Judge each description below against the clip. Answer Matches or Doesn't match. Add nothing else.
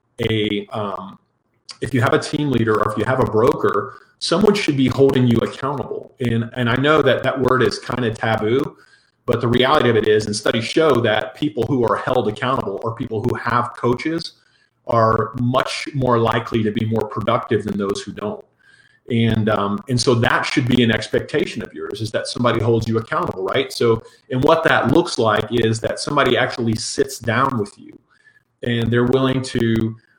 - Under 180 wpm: Doesn't match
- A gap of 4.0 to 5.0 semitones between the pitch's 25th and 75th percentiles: Doesn't match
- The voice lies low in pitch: Matches